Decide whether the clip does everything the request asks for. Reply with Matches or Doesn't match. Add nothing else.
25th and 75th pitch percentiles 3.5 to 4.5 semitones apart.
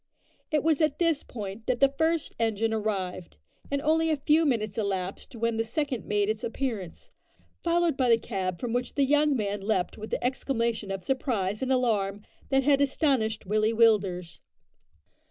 Doesn't match